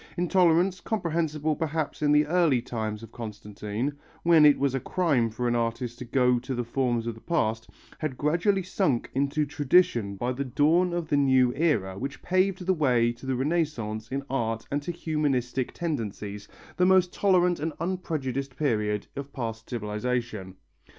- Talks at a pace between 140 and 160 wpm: No, average, 170 wpm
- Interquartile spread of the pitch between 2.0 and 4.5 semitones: No, wide, 5.6 semitones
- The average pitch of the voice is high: No, low, 135 Hz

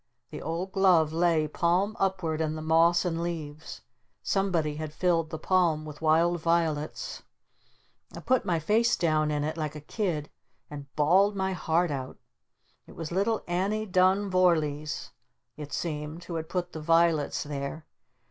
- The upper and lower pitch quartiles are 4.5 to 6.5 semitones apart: No, average, 2.9 semitones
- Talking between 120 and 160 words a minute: Yes, average, 155 wpm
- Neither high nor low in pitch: Yes, medium, 165 Hz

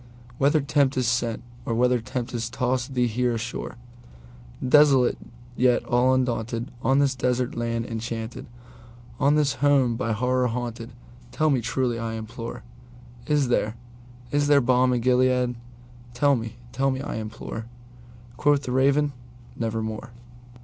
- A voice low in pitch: Yes, low, 120 Hz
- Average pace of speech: No, slow, 115 wpm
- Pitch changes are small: Yes, narrow, 1.7 semitones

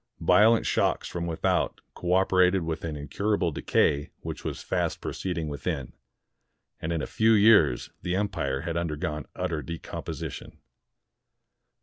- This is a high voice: No, very low, 85 Hz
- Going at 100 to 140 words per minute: Yes, slow, 135 wpm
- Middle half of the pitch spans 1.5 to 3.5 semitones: No, average, 3.9 semitones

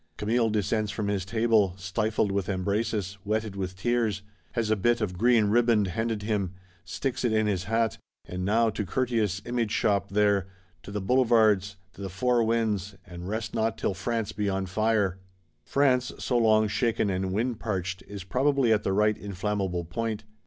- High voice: No, low, 105 Hz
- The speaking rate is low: No, average, 175 wpm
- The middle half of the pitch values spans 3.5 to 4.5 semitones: No, average, 2.7 semitones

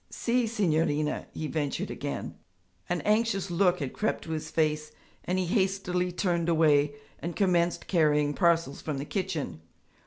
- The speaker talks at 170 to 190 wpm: No, average, 150 wpm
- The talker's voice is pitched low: No, medium, 170 Hz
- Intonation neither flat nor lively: Yes, average, 3.6 semitones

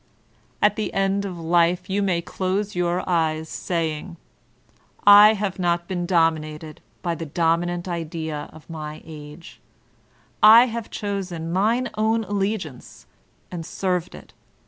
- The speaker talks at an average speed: No, slow, 130 wpm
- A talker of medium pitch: Yes, medium, 175 Hz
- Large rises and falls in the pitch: No, average, 3.4 semitones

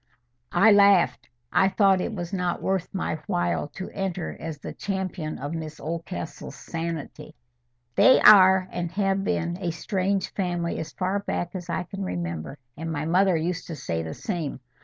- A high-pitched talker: No, medium, 175 Hz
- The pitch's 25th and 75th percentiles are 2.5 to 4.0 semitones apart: Yes, average, 3.1 semitones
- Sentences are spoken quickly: No, average, 170 wpm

